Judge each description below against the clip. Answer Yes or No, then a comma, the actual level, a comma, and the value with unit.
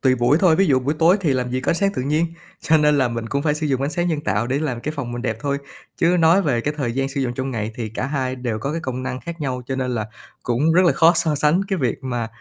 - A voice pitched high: No, low, 135 Hz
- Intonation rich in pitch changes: No, average, 4.2 semitones